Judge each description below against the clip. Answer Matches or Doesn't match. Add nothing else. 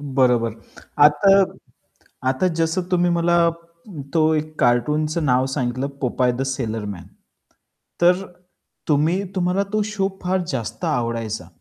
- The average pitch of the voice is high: Doesn't match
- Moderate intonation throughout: Doesn't match